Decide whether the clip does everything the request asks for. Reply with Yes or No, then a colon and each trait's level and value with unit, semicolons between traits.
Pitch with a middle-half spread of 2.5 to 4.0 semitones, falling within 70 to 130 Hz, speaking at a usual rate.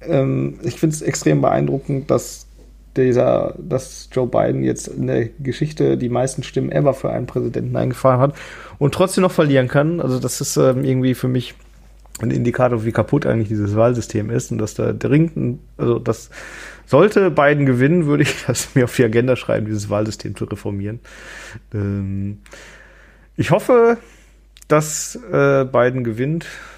No: average, 4.4 semitones; low, 125 Hz; average, 150 wpm